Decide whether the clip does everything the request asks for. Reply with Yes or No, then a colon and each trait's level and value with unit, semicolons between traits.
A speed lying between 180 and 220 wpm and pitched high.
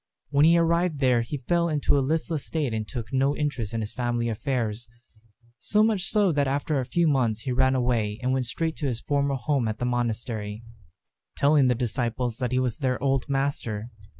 No: fast, 205 wpm; low, 130 Hz